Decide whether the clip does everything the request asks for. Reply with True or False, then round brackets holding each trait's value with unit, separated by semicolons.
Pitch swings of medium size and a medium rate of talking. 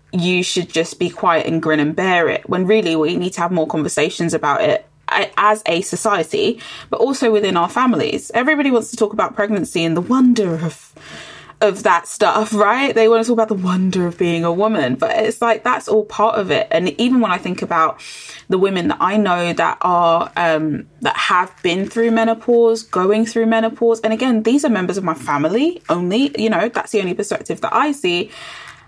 False (4.5 semitones; 210 wpm)